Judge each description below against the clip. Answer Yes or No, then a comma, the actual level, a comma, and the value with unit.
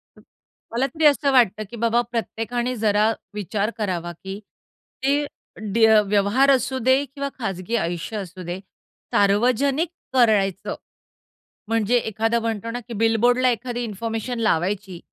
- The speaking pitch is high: Yes, high, 225 Hz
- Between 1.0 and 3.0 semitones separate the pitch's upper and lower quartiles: No, average, 3.6 semitones